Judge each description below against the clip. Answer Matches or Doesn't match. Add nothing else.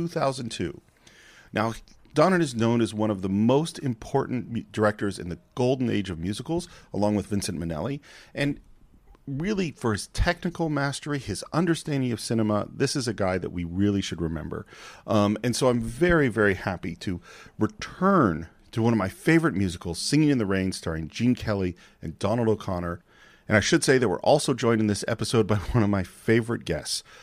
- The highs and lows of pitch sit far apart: Matches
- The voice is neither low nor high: Doesn't match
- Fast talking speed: Doesn't match